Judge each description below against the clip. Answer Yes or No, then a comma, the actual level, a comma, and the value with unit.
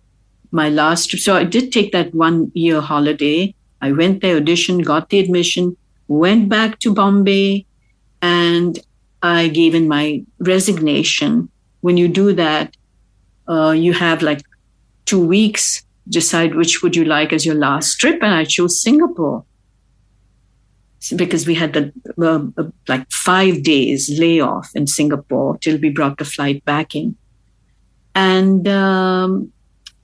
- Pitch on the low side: No, medium, 165 Hz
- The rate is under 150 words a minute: Yes, average, 140 wpm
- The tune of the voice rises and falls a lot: No, average, 3.9 semitones